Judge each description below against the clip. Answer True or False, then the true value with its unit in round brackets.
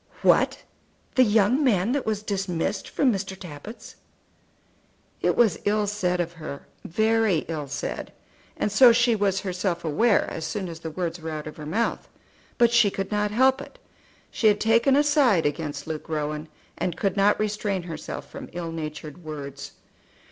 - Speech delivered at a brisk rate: False (170 wpm)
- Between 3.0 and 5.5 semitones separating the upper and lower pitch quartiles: True (5.2 semitones)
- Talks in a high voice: True (195 Hz)